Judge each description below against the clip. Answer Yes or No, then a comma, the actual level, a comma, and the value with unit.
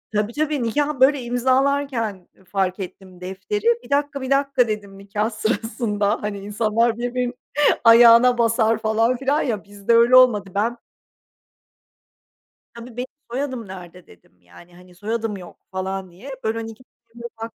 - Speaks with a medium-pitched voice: No, high, 225 Hz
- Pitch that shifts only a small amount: No, average, 3.8 semitones